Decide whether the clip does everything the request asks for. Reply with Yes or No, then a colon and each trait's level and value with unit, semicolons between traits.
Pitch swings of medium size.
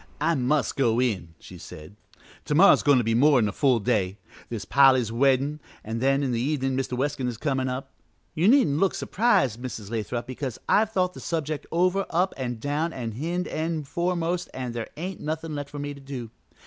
Yes: average, 4.7 semitones